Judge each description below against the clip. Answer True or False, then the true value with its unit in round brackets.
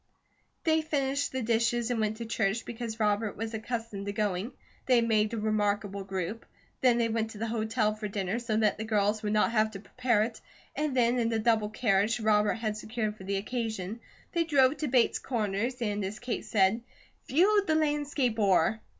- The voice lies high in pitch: True (220 Hz)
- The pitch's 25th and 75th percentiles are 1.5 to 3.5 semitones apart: True (2.4 semitones)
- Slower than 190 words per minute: False (195 wpm)